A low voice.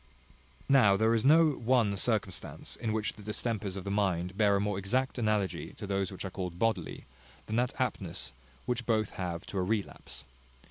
Yes: low, 105 Hz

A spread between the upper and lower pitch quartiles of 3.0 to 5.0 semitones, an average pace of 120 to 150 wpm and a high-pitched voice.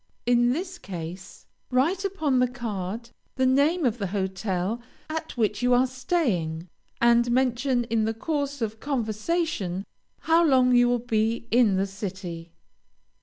Yes: average, 4.6 semitones; average, 145 wpm; high, 240 Hz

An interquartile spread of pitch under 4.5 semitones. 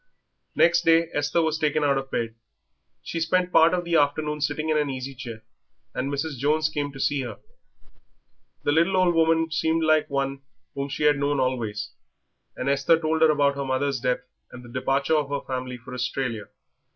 Yes: average, 3.2 semitones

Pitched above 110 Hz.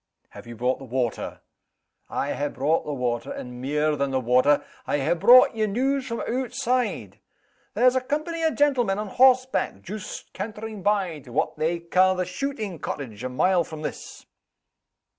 Yes: medium, 185 Hz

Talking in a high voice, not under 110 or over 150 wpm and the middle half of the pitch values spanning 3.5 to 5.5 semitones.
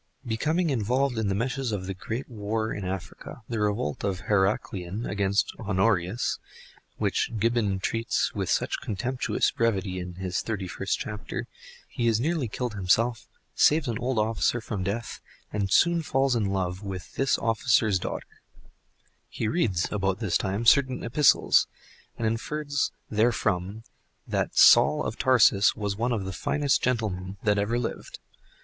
No: low, 110 Hz; average, 145 wpm; average, 3.8 semitones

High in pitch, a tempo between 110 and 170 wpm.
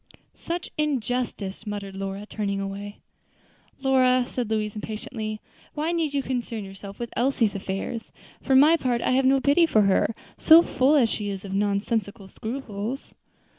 Yes: high, 225 Hz; average, 155 wpm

